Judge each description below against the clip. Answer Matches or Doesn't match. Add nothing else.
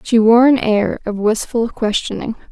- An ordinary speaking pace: Matches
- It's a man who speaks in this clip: Doesn't match